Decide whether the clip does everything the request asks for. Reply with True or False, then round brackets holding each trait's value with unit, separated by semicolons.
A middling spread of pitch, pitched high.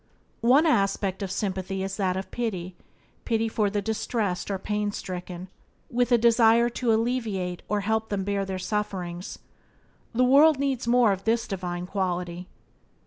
True (3.5 semitones; 205 Hz)